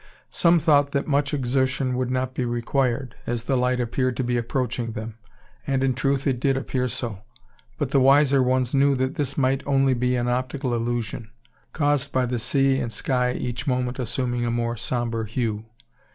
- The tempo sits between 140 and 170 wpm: No, average, 185 wpm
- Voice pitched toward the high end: No, low, 130 Hz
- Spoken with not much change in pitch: Yes, narrow, 2.2 semitones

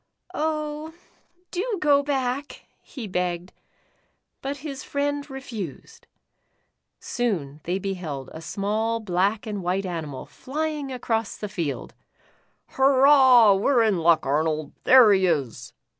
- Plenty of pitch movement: Yes, wide, 7.7 semitones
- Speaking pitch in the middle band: No, high, 220 Hz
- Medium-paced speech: No, slow, 130 wpm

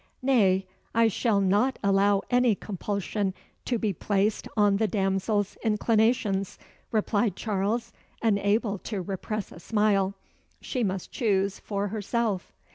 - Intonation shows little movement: Yes, narrow, 2.3 semitones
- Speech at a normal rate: No, slow, 120 wpm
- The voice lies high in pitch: Yes, high, 205 Hz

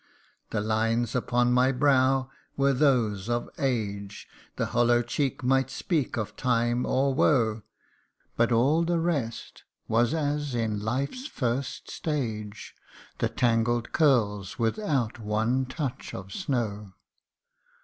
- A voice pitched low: Yes, low, 120 Hz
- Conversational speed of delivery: No, slow, 120 wpm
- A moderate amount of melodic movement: Yes, average, 3.3 semitones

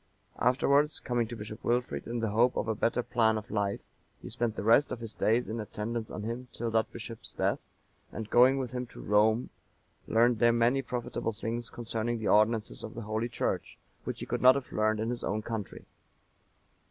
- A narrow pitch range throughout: Yes, narrow, 1.8 semitones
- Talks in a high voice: No, low, 115 Hz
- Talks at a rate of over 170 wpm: Yes, fast, 205 wpm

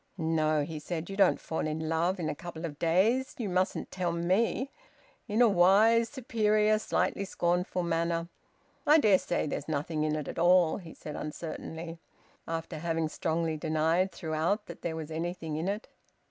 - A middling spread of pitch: Yes, average, 3.4 semitones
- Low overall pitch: No, medium, 170 Hz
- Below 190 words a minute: Yes, average, 175 wpm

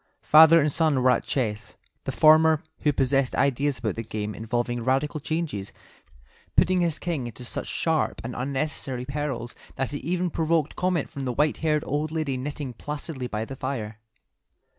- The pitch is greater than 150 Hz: No, medium, 140 Hz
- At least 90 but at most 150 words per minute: No, average, 170 wpm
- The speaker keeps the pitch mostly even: No, average, 4.0 semitones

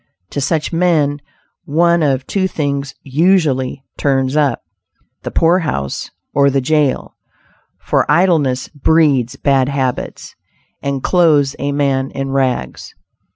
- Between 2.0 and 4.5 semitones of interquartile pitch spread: Yes, average, 3.1 semitones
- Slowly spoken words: Yes, slow, 115 wpm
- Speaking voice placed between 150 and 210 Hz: No, medium, 140 Hz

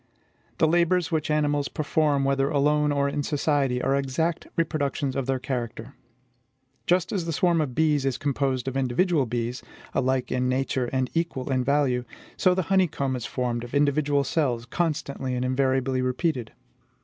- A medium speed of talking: Yes, average, 160 wpm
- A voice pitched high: No, medium, 140 Hz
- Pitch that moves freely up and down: No, average, 3.0 semitones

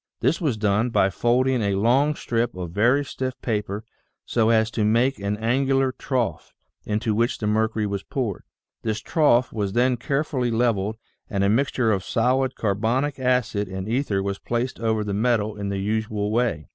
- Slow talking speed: No, average, 175 wpm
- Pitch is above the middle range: No, low, 115 Hz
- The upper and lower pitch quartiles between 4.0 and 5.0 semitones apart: No, average, 3.4 semitones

